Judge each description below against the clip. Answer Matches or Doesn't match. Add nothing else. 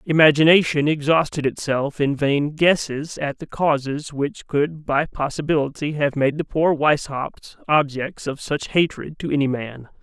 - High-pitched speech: Doesn't match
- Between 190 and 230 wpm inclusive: Doesn't match